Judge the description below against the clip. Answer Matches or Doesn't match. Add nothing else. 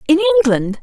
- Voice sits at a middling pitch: Doesn't match